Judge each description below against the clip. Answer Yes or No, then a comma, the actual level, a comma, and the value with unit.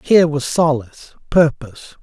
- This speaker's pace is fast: No, slow, 120 wpm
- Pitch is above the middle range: No, medium, 145 Hz